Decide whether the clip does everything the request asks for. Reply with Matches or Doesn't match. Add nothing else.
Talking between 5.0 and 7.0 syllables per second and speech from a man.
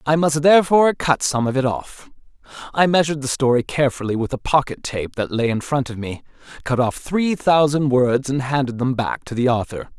Matches